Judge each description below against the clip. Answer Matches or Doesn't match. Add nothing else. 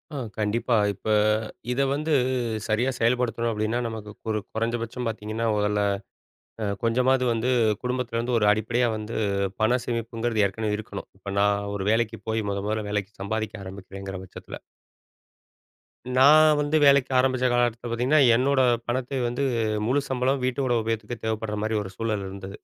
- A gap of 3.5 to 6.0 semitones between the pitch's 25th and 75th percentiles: Doesn't match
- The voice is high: Doesn't match